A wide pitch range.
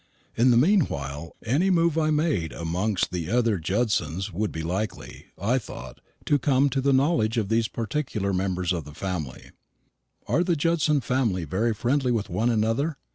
Yes: wide, 7.1 semitones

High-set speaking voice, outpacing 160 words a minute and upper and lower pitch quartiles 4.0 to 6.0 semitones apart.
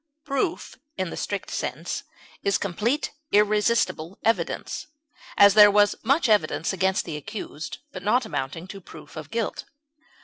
No: high, 200 Hz; average, 140 wpm; average, 4.5 semitones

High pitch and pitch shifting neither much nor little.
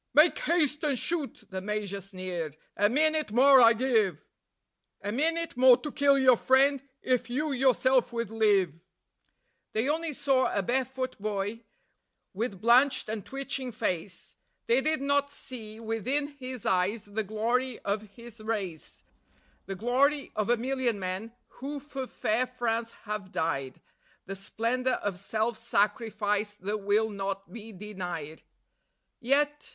Yes: high, 230 Hz; average, 4.5 semitones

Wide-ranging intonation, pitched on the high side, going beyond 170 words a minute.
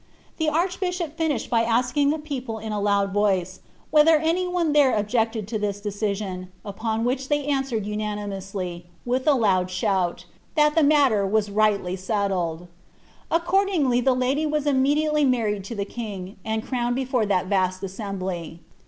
No: wide, 6.4 semitones; high, 225 Hz; average, 160 wpm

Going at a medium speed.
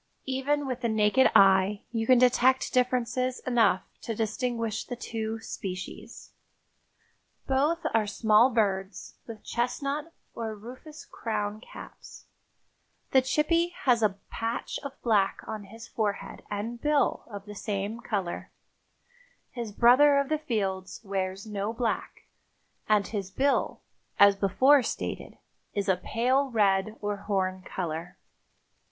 No: slow, 130 wpm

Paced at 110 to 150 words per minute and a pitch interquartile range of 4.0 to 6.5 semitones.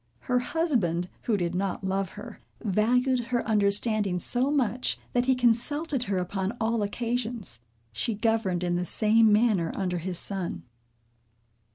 Yes: average, 145 wpm; average, 4.3 semitones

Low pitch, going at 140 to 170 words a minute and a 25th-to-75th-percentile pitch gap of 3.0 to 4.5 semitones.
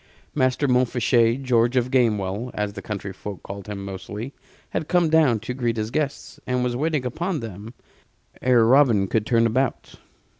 Yes: low, 120 Hz; average, 165 wpm; average, 3.5 semitones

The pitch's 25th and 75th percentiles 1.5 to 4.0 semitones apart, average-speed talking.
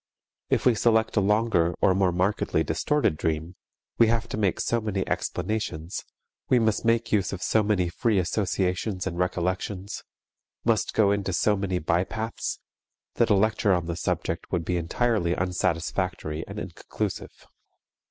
Yes: average, 3.7 semitones; average, 150 wpm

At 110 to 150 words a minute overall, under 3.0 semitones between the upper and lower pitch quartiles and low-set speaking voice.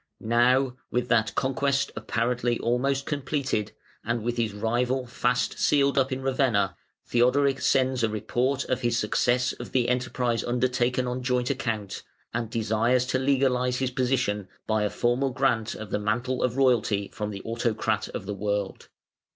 No: average, 160 wpm; narrow, 2.5 semitones; low, 125 Hz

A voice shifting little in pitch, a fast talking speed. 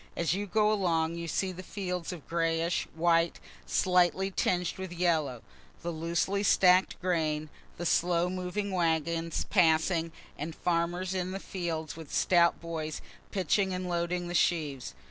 No: narrow, 1.9 semitones; average, 145 wpm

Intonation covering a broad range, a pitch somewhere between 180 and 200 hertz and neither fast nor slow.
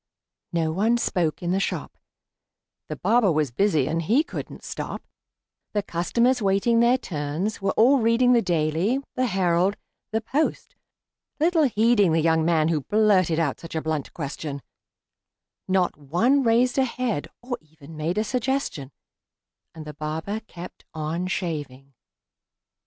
Yes: wide, 6.6 semitones; medium, 185 Hz; average, 145 wpm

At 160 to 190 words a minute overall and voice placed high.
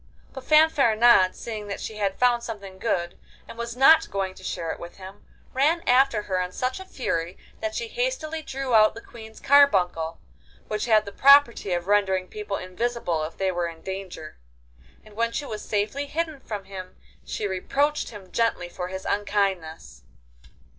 Yes: average, 175 wpm; high, 210 Hz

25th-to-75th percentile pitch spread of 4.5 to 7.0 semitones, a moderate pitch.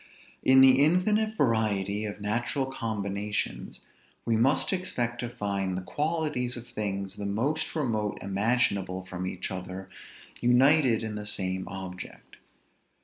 No: average, 5.1 semitones; low, 110 Hz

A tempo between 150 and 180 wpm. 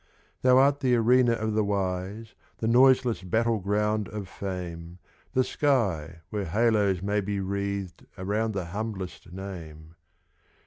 No: slow, 135 wpm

